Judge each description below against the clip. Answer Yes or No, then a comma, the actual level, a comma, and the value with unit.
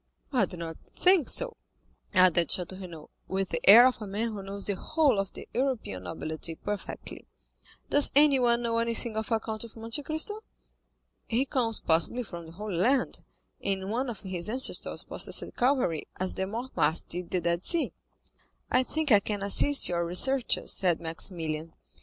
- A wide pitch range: Yes, wide, 5.9 semitones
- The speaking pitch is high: Yes, high, 210 Hz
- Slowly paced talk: No, average, 170 wpm